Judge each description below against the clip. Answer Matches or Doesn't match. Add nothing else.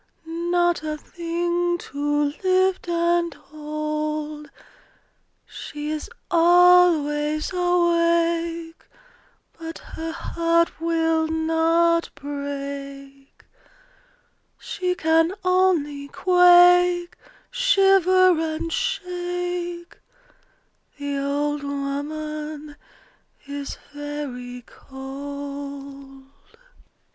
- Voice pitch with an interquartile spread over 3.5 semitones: Doesn't match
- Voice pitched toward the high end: Matches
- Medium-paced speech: Doesn't match